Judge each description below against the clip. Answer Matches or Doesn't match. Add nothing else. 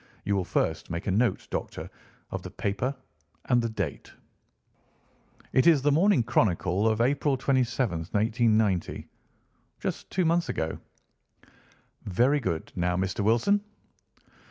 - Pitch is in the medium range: Doesn't match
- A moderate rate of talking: Doesn't match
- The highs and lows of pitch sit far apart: Matches